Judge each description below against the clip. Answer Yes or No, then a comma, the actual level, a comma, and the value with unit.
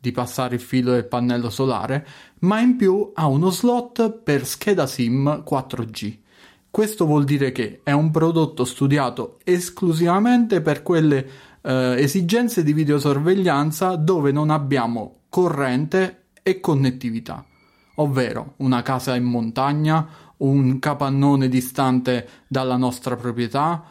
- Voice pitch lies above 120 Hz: Yes, medium, 140 Hz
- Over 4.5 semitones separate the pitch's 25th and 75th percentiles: Yes, average, 5.0 semitones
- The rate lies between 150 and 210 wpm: No, average, 125 wpm